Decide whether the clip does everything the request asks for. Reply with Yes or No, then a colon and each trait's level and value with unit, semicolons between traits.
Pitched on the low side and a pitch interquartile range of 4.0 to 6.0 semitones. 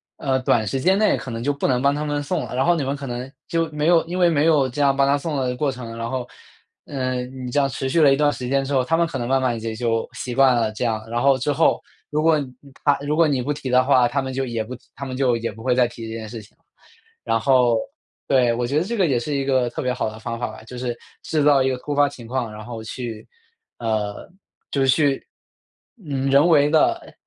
No: low, 130 Hz; average, 3.0 semitones